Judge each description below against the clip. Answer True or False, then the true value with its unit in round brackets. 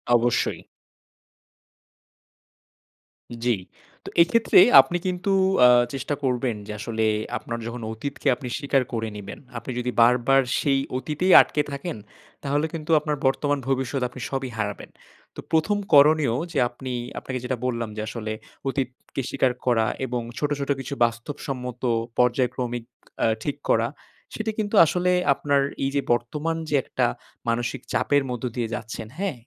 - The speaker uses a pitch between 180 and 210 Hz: False (130 Hz)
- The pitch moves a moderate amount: True (3.3 semitones)